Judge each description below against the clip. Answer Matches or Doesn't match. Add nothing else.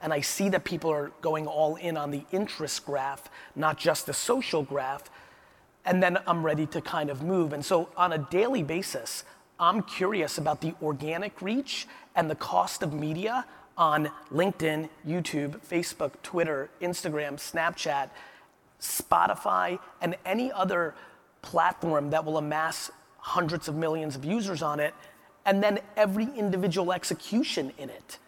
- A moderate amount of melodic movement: Matches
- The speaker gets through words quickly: Doesn't match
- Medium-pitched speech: Matches